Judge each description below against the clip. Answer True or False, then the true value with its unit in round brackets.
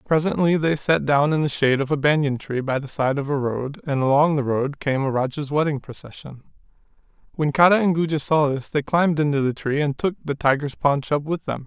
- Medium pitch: True (145 Hz)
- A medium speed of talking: False (230 wpm)